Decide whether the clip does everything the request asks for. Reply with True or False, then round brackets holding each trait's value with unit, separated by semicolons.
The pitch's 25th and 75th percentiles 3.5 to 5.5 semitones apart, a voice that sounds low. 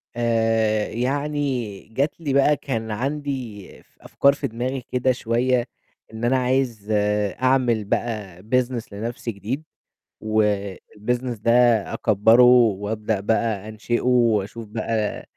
False (2.9 semitones; 115 Hz)